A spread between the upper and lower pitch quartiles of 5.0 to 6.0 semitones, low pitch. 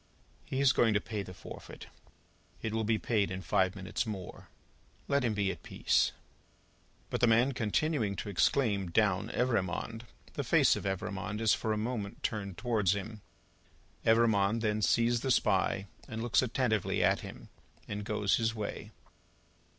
No: average, 2.7 semitones; low, 110 Hz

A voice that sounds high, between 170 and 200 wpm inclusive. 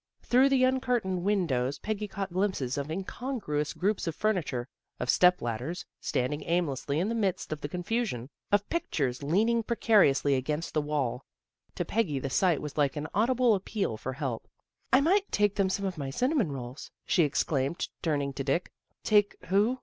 No: medium, 175 Hz; average, 185 wpm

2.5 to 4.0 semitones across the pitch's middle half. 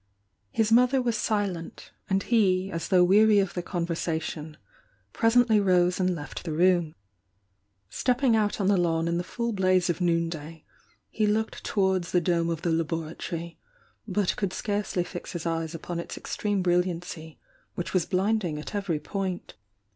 Yes: average, 3.4 semitones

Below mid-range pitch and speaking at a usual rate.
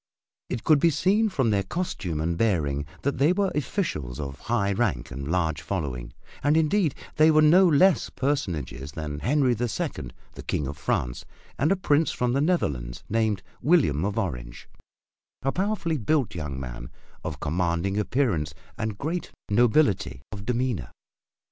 Yes: low, 105 Hz; average, 160 wpm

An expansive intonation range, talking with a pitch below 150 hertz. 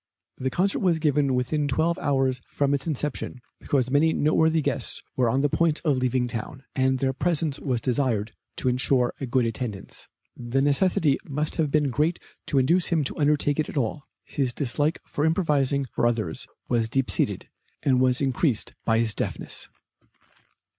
No: average, 3.1 semitones; low, 135 Hz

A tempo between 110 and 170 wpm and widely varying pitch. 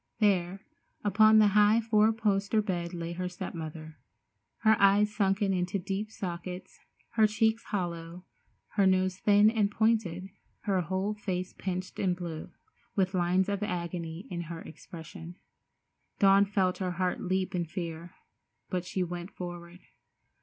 No: average, 145 wpm; average, 2.9 semitones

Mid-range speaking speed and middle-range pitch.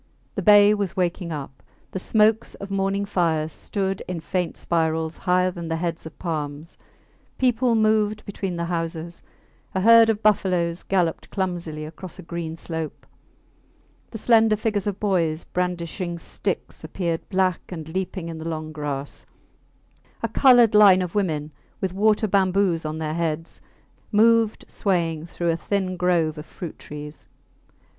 Yes: average, 150 wpm; medium, 180 Hz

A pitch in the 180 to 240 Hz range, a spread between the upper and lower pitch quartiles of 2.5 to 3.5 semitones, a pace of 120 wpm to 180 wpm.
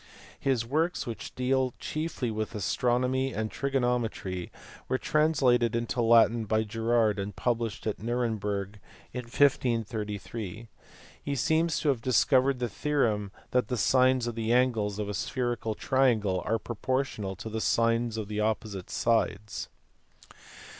No: low, 115 Hz; average, 3.0 semitones; average, 140 wpm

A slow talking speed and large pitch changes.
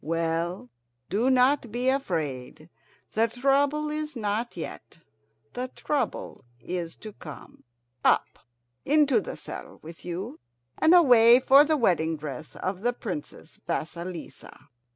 Yes: slow, 125 wpm; wide, 8.0 semitones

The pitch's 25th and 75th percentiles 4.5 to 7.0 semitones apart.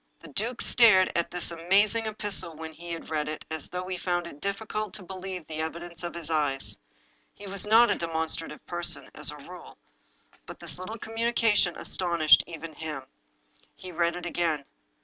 No: average, 3.5 semitones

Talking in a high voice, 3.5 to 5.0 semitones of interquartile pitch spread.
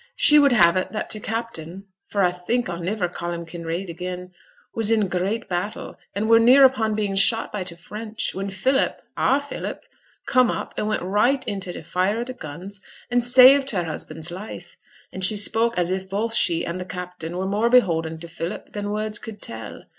Yes: high, 200 Hz; average, 4.2 semitones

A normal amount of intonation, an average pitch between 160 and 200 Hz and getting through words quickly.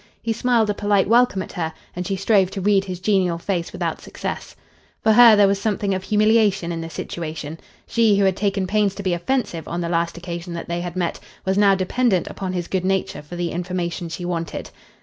Yes: average, 3.0 semitones; high, 190 Hz; fast, 220 wpm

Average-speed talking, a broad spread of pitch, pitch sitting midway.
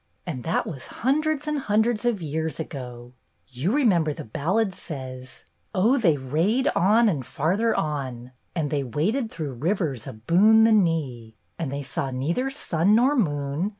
Yes: average, 170 wpm; wide, 8.2 semitones; medium, 165 Hz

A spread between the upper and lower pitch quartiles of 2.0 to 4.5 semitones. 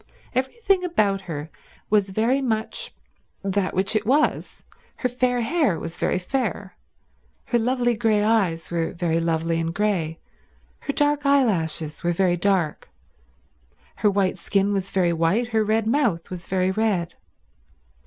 No: wide, 5.6 semitones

